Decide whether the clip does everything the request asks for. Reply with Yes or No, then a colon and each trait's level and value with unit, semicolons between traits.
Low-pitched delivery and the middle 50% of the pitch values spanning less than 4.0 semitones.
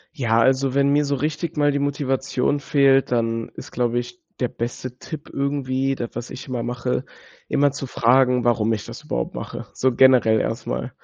Yes: low, 130 Hz; narrow, 2.5 semitones